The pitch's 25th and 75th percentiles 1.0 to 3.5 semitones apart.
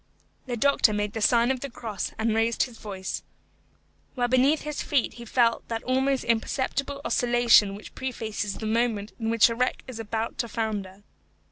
Yes: narrow, 2.6 semitones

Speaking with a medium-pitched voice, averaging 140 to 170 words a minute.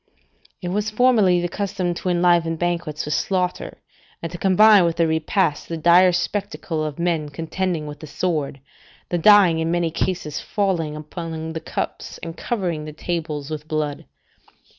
Yes: medium, 170 Hz; average, 160 wpm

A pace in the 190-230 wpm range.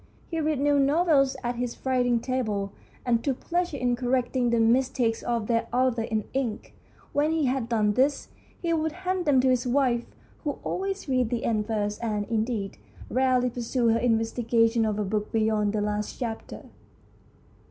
No: average, 175 wpm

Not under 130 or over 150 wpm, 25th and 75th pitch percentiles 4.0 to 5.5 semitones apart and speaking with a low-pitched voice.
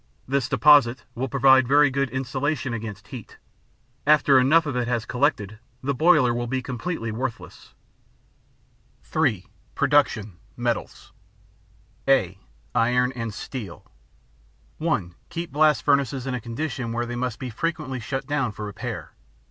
No: slow, 135 wpm; average, 3.2 semitones; low, 130 Hz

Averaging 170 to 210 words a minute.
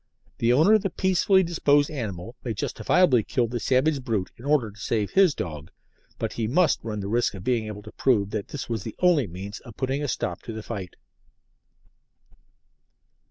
Yes: average, 195 wpm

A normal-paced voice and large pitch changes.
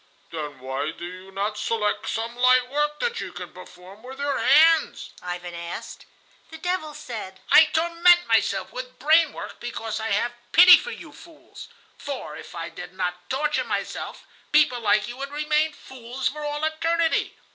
Yes: average, 170 wpm; wide, 7.5 semitones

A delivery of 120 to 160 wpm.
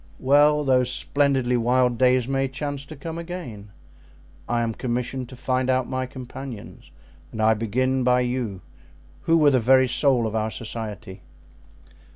Yes: average, 155 wpm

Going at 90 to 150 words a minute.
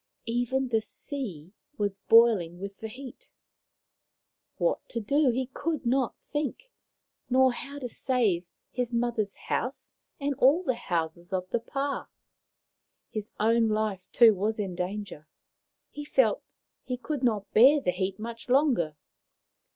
Yes: average, 140 wpm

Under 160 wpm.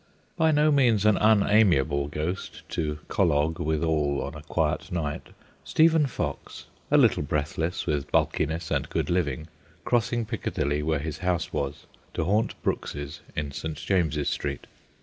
Yes: average, 145 wpm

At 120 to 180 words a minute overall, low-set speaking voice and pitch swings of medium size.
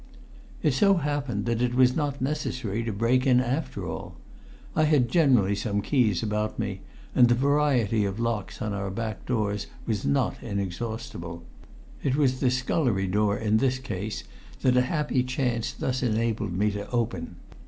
Yes: average, 165 wpm; low, 115 Hz; average, 3.9 semitones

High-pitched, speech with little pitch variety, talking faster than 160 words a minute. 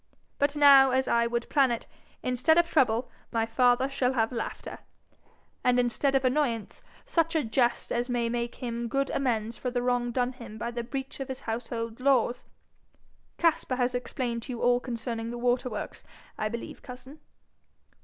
Yes: high, 245 Hz; narrow, 2.1 semitones; average, 175 wpm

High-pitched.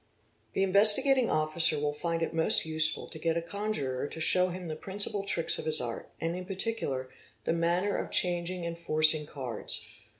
No: medium, 170 Hz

